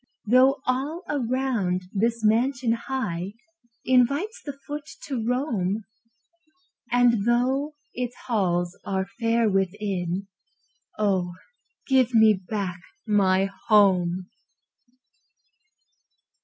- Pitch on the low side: No, high, 225 Hz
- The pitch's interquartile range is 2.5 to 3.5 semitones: No, average, 5.0 semitones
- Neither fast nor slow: No, slow, 90 wpm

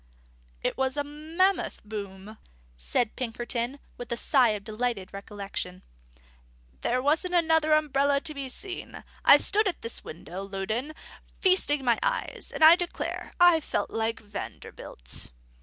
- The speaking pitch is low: No, very high, 255 Hz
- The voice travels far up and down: Yes, wide, 6.6 semitones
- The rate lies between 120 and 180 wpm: Yes, average, 140 wpm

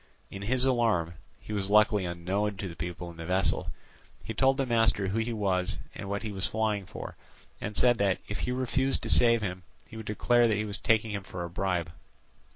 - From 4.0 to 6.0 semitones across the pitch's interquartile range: No, average, 3.5 semitones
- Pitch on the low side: Yes, low, 105 Hz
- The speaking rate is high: Yes, fast, 210 wpm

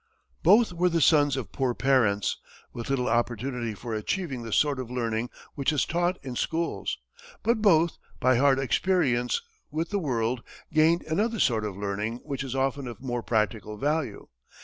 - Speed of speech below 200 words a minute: Yes, average, 170 wpm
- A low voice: Yes, low, 130 Hz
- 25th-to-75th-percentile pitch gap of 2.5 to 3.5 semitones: No, average, 5.2 semitones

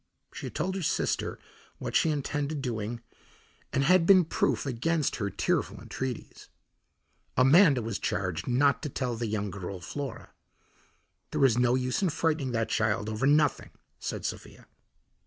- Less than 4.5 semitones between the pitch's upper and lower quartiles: No, average, 4.8 semitones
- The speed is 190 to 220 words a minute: No, average, 155 wpm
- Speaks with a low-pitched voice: Yes, low, 130 Hz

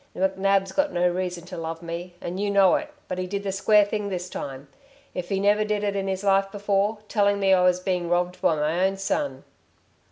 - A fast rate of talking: Yes, fast, 225 wpm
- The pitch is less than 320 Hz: Yes, high, 190 Hz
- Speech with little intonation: Yes, narrow, 2.1 semitones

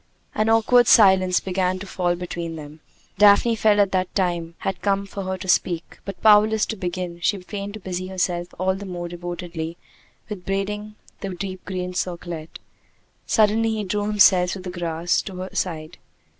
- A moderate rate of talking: Yes, average, 175 wpm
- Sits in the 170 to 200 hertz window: Yes, medium, 185 Hz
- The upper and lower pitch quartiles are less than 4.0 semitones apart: Yes, narrow, 2.5 semitones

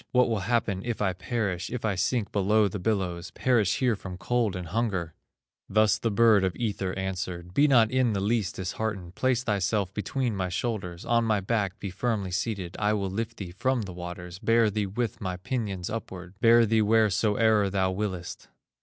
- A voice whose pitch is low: Yes, low, 105 Hz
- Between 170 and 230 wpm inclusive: Yes, average, 190 wpm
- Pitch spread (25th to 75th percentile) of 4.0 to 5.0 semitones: No, average, 3.5 semitones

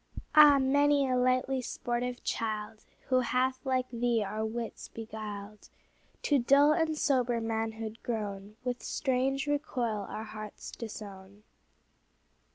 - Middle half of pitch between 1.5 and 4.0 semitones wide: Yes, average, 3.3 semitones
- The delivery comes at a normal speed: No, slow, 120 wpm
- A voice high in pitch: Yes, high, 240 Hz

